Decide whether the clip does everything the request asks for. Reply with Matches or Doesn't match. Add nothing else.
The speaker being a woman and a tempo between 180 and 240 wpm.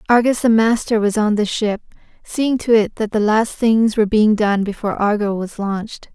Matches